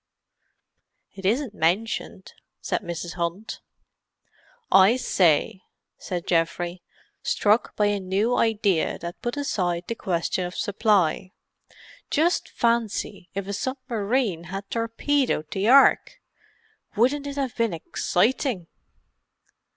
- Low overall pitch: No, high, 205 Hz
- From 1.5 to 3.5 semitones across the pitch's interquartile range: No, average, 4.8 semitones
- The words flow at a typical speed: No, slow, 110 wpm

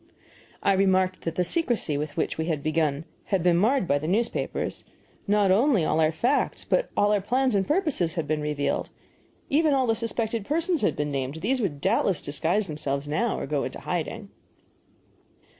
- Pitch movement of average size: No, wide, 6.9 semitones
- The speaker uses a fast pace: No, average, 185 wpm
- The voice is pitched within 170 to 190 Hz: Yes, medium, 185 Hz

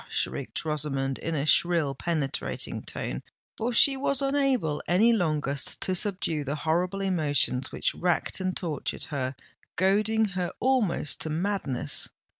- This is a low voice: No, medium, 170 Hz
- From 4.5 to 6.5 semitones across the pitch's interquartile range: Yes, wide, 5.4 semitones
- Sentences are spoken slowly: Yes, slow, 130 wpm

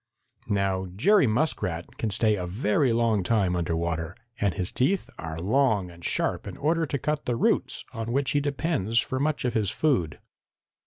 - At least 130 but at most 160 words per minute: No, average, 180 wpm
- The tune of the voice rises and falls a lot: Yes, wide, 7.2 semitones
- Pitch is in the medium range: No, low, 110 Hz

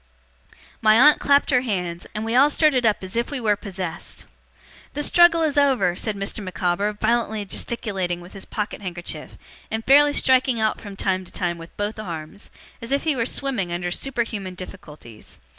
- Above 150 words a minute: Yes, average, 180 wpm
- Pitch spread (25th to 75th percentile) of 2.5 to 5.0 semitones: No, wide, 5.6 semitones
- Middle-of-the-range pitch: No, high, 210 Hz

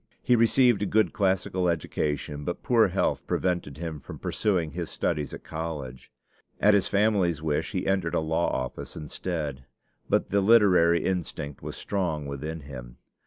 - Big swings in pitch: No, average, 4.8 semitones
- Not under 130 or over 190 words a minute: Yes, average, 160 wpm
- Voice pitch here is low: Yes, very low, 85 Hz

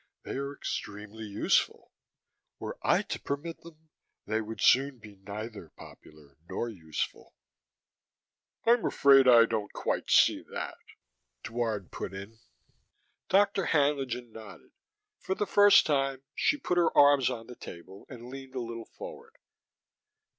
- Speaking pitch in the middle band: No, low, 125 Hz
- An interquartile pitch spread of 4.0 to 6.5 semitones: Yes, average, 5.0 semitones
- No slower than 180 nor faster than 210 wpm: No, slow, 135 wpm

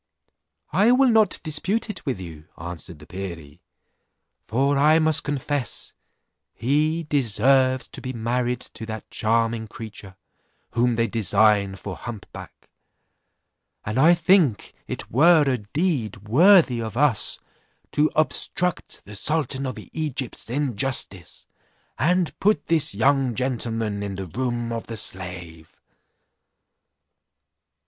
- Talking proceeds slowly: Yes, slow, 125 wpm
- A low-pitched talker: Yes, low, 120 Hz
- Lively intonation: Yes, wide, 6.1 semitones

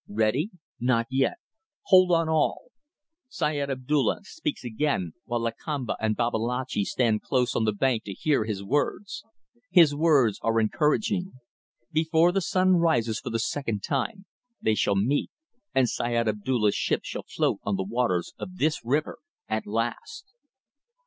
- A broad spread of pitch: Yes, wide, 6.2 semitones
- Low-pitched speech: Yes, low, 130 Hz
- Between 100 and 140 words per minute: No, average, 150 wpm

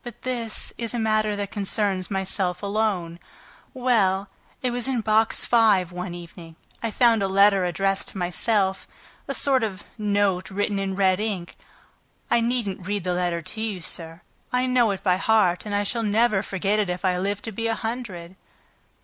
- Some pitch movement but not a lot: Yes, average, 3.1 semitones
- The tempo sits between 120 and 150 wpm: No, average, 185 wpm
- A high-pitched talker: Yes, high, 205 Hz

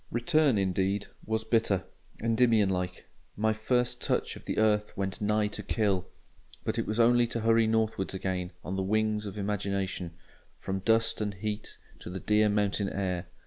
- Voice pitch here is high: No, low, 105 Hz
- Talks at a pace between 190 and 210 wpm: No, average, 170 wpm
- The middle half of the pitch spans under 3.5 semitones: Yes, narrow, 2.5 semitones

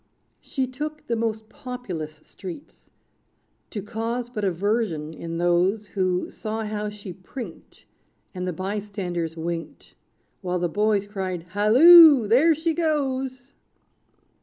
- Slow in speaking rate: Yes, slow, 120 wpm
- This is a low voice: No, high, 210 Hz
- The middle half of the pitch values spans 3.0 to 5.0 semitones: No, wide, 5.5 semitones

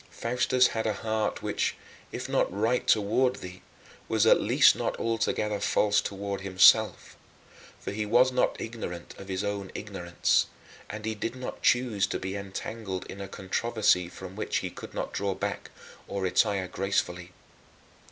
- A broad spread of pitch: No, average, 2.7 semitones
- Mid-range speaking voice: No, low, 100 Hz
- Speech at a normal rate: Yes, average, 160 wpm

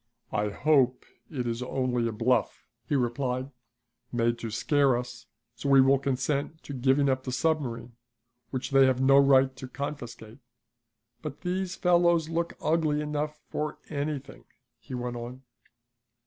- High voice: No, low, 135 Hz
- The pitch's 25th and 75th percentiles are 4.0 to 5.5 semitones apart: No, average, 3.2 semitones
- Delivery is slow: No, average, 150 wpm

